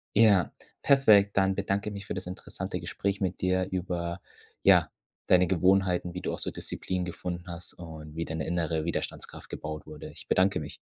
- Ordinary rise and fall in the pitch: No, narrow, 2.3 semitones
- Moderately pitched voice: No, very low, 90 Hz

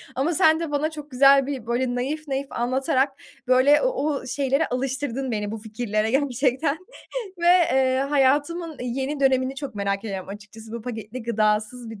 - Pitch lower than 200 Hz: No, very high, 260 Hz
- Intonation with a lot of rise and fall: No, average, 3.5 semitones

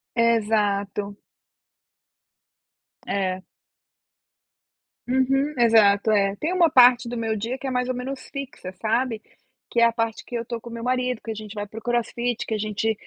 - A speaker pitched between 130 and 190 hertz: No, high, 230 Hz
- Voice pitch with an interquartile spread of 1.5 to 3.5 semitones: Yes, average, 2.8 semitones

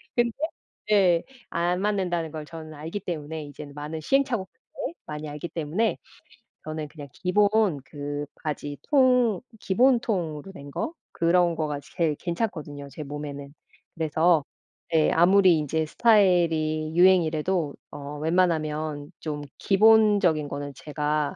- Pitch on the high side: No, medium, 160 Hz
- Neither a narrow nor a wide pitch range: Yes, average, 4.0 semitones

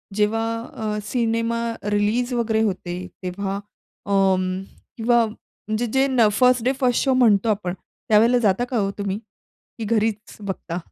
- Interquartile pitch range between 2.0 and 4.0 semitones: Yes, average, 2.9 semitones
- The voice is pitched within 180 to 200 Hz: No, high, 215 Hz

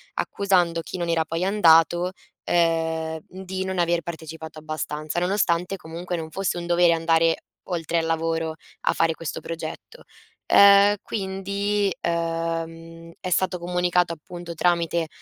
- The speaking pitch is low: No, medium, 170 Hz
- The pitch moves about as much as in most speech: No, narrow, 1.7 semitones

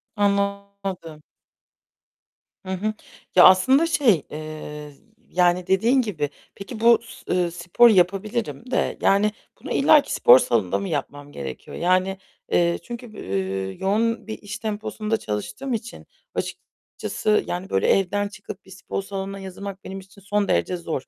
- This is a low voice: No, high, 195 Hz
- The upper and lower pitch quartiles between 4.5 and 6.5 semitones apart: No, average, 3.5 semitones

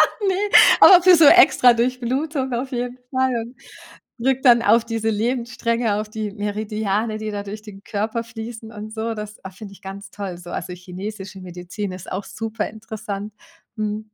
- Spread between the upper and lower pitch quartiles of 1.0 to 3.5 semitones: Yes, average, 2.8 semitones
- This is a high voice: Yes, high, 220 Hz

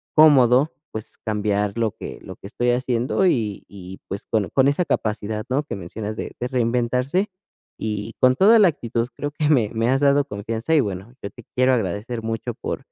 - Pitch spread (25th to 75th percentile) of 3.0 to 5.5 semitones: Yes, average, 4.1 semitones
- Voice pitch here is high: No, low, 120 Hz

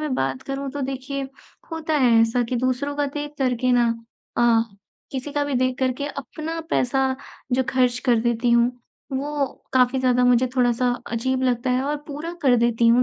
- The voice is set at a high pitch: Yes, very high, 255 Hz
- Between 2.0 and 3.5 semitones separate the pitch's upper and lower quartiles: Yes, narrow, 2.4 semitones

